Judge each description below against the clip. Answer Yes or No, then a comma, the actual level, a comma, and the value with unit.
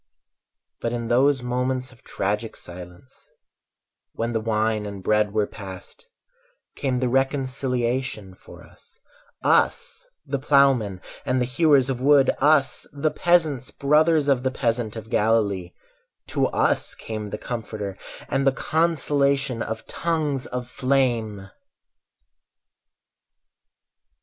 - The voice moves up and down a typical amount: Yes, average, 4.1 semitones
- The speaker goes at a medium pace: No, slow, 120 wpm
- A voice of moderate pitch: No, low, 125 Hz